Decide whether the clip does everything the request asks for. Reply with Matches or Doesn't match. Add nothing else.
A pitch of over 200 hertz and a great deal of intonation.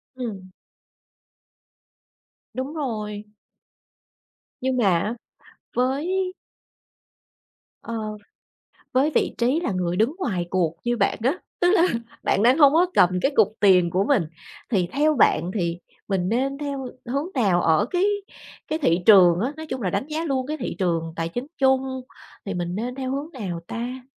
Matches